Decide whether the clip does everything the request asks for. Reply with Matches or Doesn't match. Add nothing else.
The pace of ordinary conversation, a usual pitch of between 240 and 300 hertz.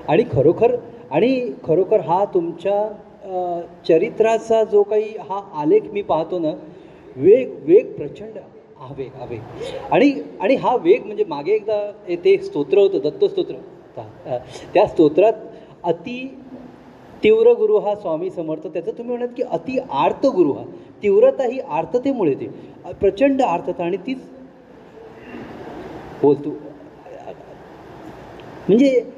Matches